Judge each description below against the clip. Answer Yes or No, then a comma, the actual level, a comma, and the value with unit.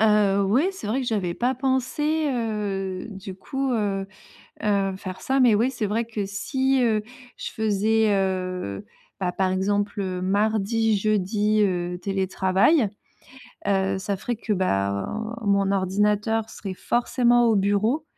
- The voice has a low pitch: No, high, 205 Hz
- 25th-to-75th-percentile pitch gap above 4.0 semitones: No, average, 3.0 semitones